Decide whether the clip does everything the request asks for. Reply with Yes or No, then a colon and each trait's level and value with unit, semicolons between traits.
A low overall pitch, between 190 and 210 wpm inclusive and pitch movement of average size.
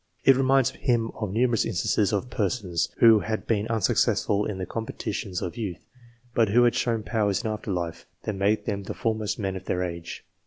Yes: low, 105 Hz; average, 195 wpm; average, 3.0 semitones